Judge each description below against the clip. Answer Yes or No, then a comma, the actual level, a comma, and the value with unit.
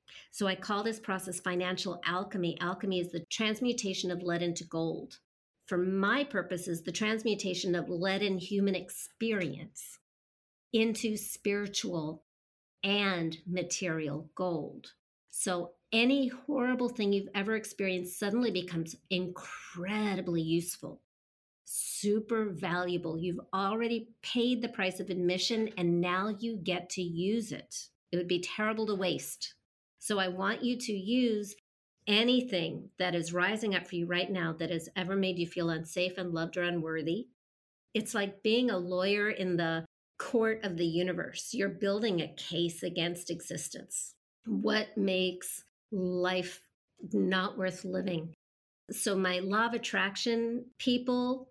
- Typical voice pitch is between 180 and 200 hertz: Yes, medium, 185 Hz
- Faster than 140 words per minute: No, slow, 135 wpm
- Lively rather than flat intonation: No, average, 3.4 semitones